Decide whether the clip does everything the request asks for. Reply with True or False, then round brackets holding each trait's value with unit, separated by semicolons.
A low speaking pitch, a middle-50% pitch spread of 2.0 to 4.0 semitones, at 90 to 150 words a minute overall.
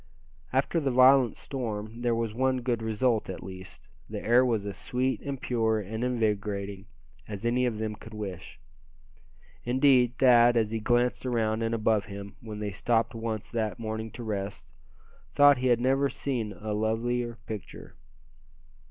False (115 Hz; 2.7 semitones; 160 wpm)